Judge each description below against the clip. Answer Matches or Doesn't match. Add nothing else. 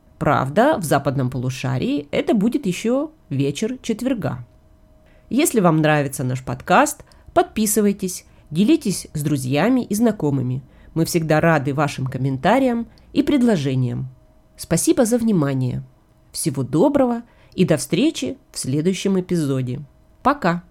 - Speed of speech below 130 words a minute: Matches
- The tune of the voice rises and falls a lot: Matches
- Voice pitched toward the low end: Doesn't match